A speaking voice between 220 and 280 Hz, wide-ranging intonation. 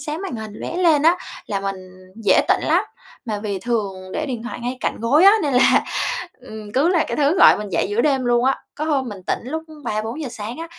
Yes: high, 245 Hz; wide, 6.2 semitones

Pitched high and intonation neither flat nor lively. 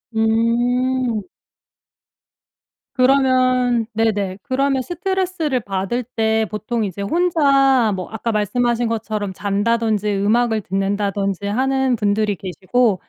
Yes: high, 225 Hz; average, 3.7 semitones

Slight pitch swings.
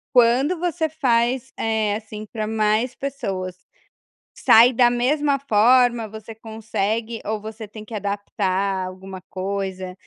No: average, 3.3 semitones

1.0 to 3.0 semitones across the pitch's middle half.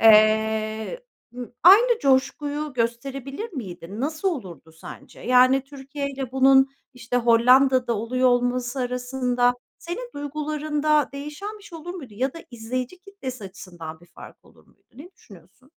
No: average, 4.2 semitones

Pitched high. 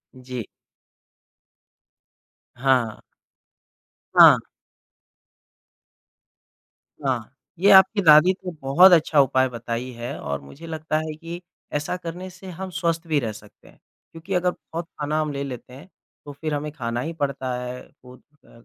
No: medium, 150 Hz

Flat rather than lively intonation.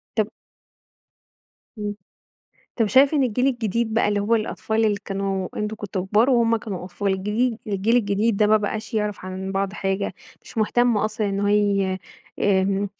Yes: narrow, 2.2 semitones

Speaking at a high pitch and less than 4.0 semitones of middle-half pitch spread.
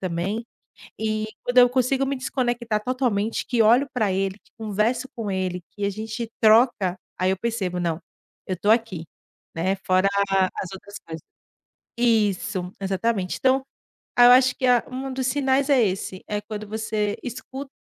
No: high, 220 Hz; average, 4.4 semitones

